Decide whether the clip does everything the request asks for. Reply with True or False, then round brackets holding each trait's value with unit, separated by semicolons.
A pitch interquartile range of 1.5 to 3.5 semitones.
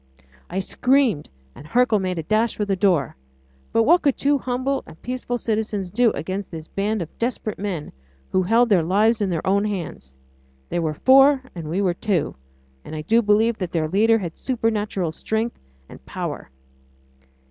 False (4.8 semitones)